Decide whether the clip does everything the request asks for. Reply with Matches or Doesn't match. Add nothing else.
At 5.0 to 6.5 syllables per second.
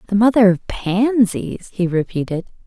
Doesn't match